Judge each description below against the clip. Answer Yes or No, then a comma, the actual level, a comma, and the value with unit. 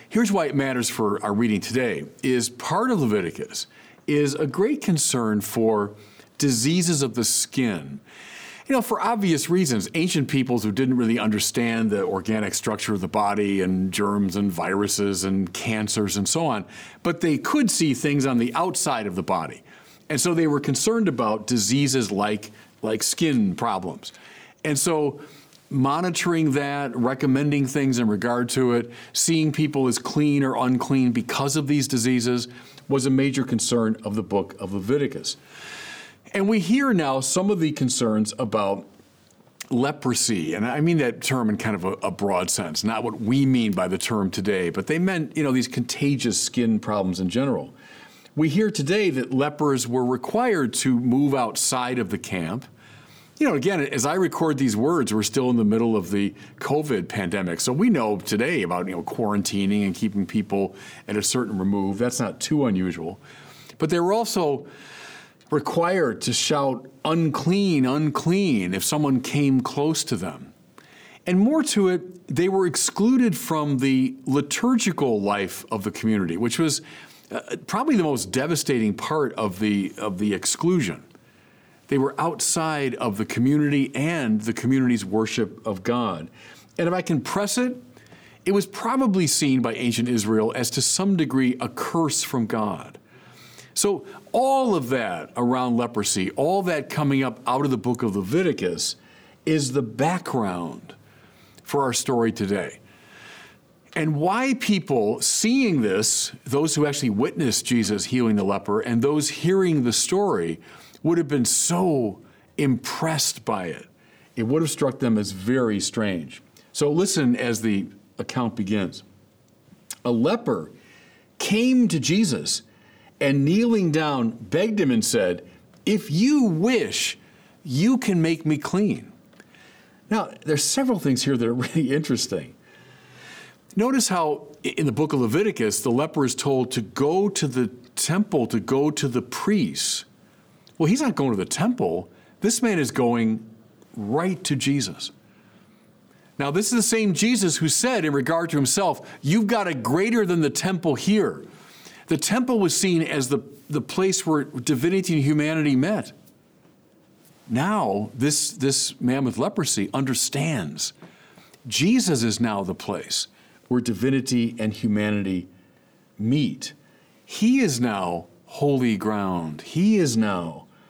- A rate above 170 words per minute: No, average, 155 wpm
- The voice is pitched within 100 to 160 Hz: Yes, low, 135 Hz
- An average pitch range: No, wide, 6.3 semitones